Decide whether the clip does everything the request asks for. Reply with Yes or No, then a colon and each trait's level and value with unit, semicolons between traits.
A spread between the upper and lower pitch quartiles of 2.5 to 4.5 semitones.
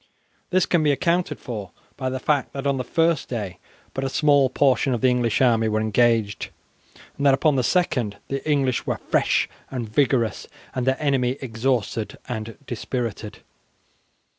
Yes: average, 3.4 semitones